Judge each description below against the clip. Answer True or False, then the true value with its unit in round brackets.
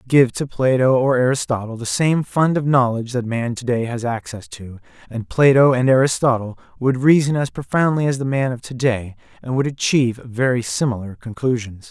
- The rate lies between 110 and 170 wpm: False (185 wpm)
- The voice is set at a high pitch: False (125 Hz)